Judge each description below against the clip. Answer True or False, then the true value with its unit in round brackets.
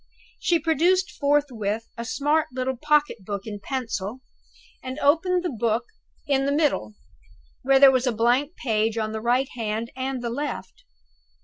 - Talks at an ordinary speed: True (155 wpm)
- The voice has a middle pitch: False (255 Hz)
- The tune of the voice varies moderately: True (4.5 semitones)